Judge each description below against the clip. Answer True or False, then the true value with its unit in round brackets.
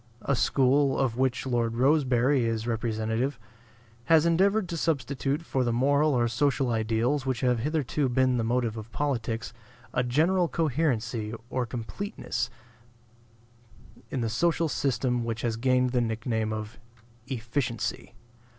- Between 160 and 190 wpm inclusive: False (140 wpm)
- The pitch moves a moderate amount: True (3.7 semitones)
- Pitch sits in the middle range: False (125 Hz)